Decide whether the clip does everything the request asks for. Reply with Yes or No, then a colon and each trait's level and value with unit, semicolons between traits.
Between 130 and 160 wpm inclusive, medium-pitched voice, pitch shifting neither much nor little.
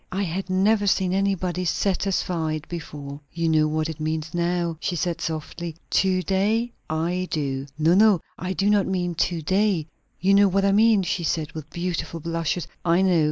No: average, 180 wpm; medium, 175 Hz; average, 3.1 semitones